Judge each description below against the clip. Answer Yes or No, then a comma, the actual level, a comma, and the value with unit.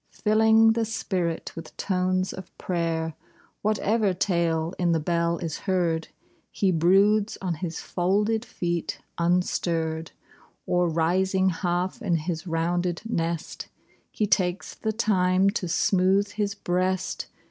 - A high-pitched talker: No, medium, 180 Hz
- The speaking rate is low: Yes, slow, 125 wpm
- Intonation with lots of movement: No, average, 2.9 semitones